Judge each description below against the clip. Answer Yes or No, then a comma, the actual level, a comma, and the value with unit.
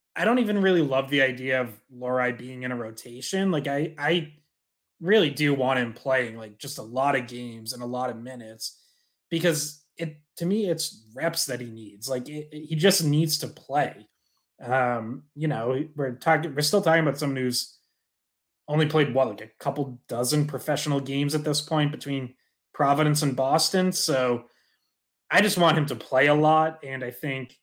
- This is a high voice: No, medium, 140 Hz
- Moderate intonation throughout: Yes, average, 3.8 semitones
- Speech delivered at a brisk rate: No, average, 190 wpm